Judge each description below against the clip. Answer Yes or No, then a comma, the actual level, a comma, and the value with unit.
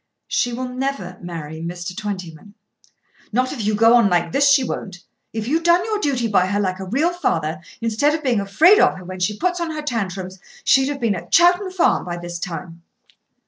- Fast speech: Yes, fast, 210 wpm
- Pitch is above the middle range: Yes, high, 215 Hz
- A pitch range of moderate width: No, wide, 7.6 semitones